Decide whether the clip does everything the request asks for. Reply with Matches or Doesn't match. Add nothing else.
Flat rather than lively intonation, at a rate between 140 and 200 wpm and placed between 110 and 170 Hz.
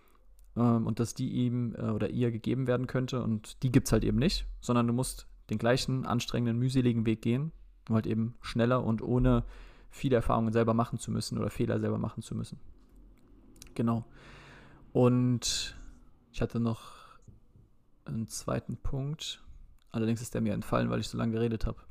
Matches